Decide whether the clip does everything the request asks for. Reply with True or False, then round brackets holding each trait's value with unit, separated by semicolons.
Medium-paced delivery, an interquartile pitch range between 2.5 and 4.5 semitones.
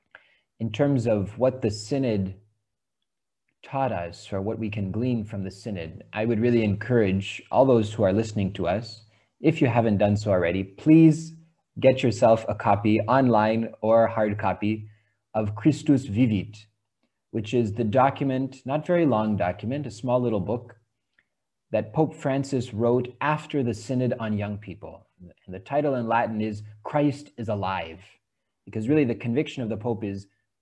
False (165 wpm; 3.7 semitones)